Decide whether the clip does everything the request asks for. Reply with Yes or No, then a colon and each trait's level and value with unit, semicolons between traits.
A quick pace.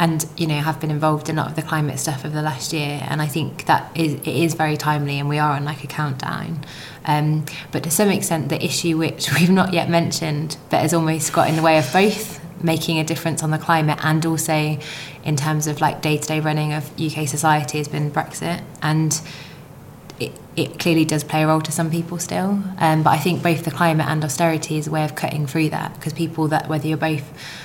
Yes: fast, 235 wpm